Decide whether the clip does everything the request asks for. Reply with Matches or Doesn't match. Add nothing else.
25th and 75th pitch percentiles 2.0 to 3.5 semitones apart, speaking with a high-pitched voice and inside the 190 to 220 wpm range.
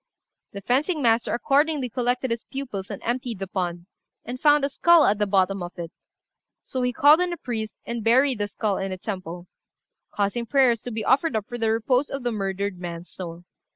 Doesn't match